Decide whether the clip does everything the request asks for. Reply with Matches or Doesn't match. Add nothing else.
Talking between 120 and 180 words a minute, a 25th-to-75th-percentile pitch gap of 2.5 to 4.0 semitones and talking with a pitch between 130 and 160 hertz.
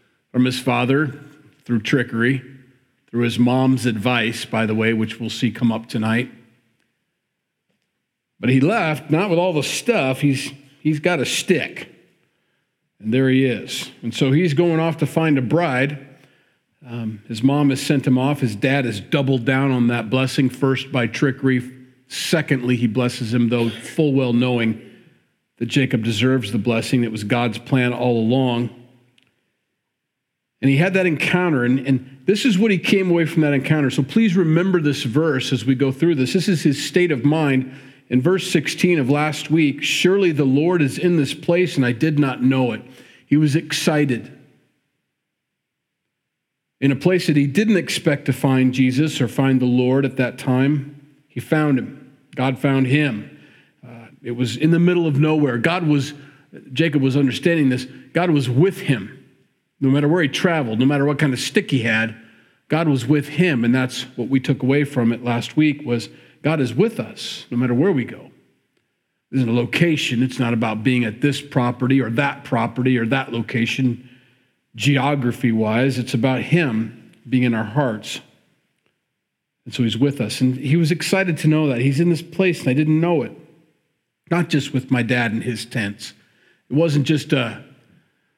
Doesn't match